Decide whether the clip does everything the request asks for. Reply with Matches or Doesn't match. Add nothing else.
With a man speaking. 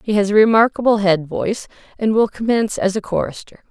Doesn't match